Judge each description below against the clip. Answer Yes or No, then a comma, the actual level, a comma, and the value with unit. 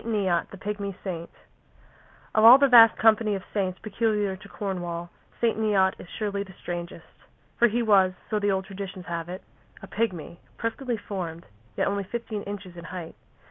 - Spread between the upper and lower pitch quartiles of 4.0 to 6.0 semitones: No, average, 2.9 semitones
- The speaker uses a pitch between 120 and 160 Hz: No, high, 200 Hz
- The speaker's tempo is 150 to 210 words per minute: Yes, average, 175 wpm